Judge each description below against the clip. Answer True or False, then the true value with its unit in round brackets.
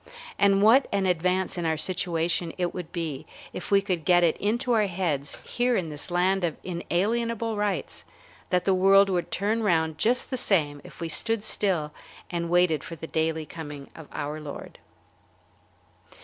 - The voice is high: False (180 Hz)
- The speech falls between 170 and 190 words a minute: True (175 wpm)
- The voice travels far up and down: False (3.8 semitones)